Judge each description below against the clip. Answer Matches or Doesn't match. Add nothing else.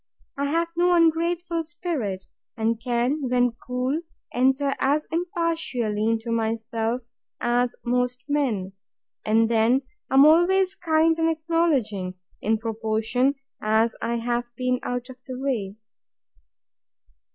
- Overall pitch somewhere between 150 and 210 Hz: Doesn't match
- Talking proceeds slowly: Matches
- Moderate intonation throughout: Doesn't match